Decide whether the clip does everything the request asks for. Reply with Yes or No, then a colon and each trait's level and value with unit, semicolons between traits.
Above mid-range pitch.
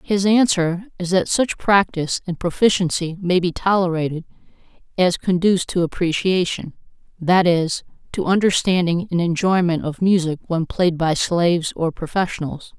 No: medium, 175 Hz